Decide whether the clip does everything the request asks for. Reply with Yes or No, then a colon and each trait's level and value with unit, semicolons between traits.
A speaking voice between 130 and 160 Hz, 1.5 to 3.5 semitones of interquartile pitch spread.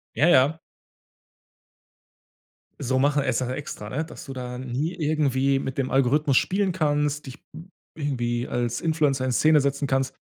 Yes: medium, 140 Hz; narrow, 2.6 semitones